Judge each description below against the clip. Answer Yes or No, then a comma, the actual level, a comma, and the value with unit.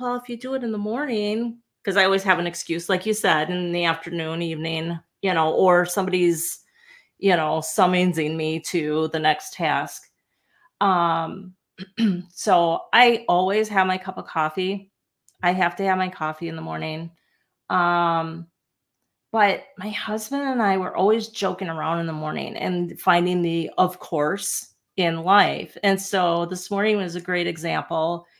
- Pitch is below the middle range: No, medium, 180 Hz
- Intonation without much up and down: No, average, 3.4 semitones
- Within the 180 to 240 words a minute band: No, average, 165 wpm